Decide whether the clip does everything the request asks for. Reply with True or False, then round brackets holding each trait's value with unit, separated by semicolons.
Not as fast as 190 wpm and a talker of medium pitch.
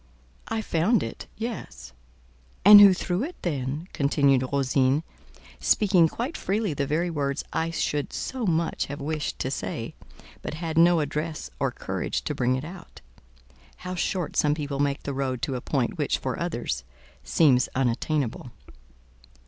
True (155 wpm; 150 Hz)